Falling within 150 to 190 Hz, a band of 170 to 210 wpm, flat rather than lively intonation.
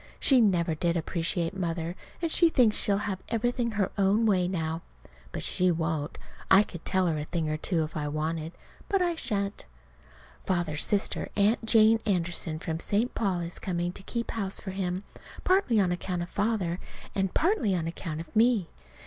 No: medium, 185 Hz; average, 185 wpm; average, 4.2 semitones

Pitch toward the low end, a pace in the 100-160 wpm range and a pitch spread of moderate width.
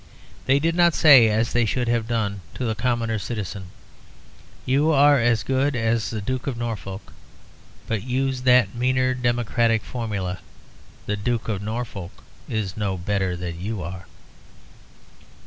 Yes: low, 115 Hz; average, 145 wpm; average, 3.7 semitones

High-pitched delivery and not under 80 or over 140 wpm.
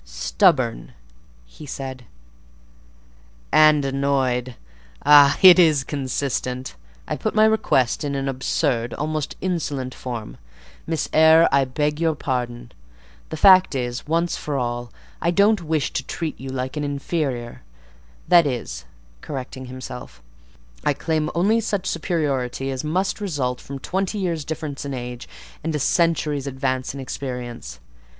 No: medium, 140 Hz; slow, 135 wpm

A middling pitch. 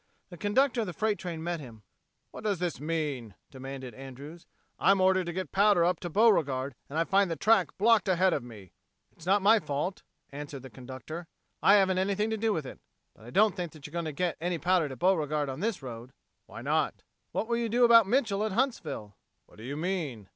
Yes: medium, 175 Hz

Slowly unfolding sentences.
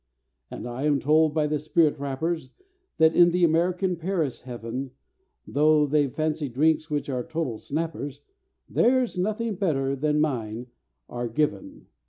No: average, 145 wpm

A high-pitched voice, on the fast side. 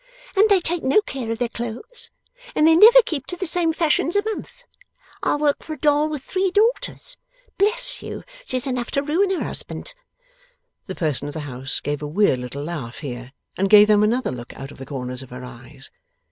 Yes: very high, 250 Hz; fast, 210 wpm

